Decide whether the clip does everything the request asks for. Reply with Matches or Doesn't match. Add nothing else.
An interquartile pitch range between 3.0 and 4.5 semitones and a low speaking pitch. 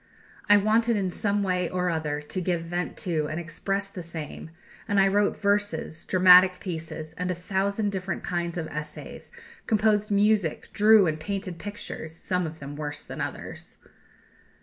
Doesn't match